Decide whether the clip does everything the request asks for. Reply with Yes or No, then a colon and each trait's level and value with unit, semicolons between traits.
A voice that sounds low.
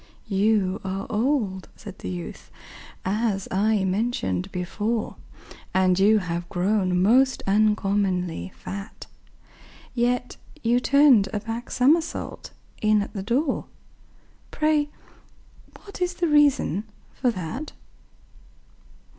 No: high, 210 Hz